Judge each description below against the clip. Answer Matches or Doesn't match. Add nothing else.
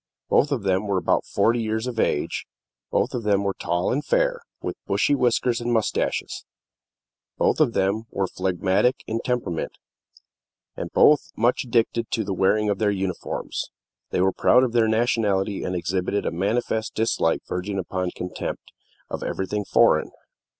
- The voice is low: Matches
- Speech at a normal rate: Matches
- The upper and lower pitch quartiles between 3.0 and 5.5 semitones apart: Matches